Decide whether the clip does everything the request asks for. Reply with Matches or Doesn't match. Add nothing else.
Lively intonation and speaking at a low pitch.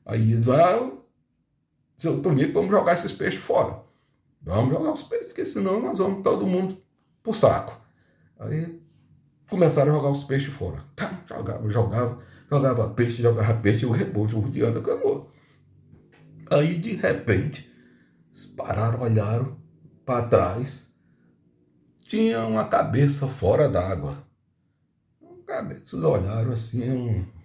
Matches